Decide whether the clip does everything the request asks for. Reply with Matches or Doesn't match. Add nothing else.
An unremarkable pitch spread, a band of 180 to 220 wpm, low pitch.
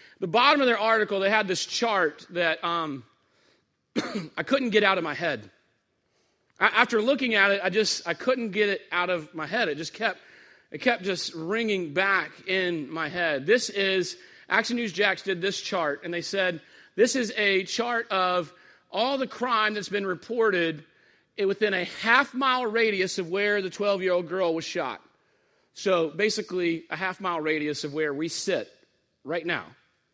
Doesn't match